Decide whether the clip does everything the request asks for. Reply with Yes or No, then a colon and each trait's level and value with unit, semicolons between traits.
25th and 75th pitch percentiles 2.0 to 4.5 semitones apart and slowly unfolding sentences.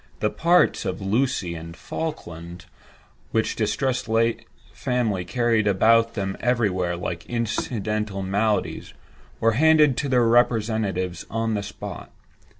Yes: average, 3.9 semitones; slow, 125 wpm